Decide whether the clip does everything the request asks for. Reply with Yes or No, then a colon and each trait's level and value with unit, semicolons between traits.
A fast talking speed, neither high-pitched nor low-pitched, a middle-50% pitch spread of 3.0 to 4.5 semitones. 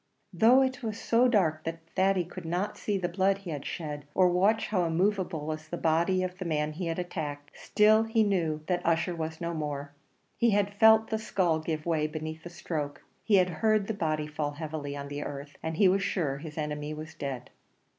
Yes: fast, 215 wpm; medium, 170 Hz; average, 4.2 semitones